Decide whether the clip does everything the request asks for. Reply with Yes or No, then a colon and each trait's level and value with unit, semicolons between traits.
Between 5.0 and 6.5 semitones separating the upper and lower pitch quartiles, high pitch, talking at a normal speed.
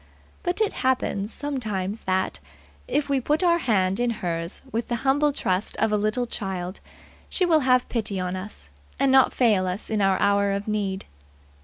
Yes: wide, 5.4 semitones; high, 215 Hz; average, 180 wpm